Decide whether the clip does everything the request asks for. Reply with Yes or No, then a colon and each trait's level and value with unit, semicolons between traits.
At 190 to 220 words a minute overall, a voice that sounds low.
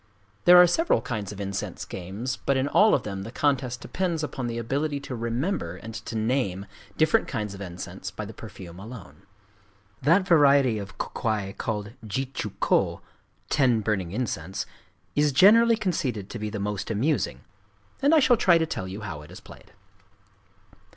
No: average, 175 wpm; low, 115 Hz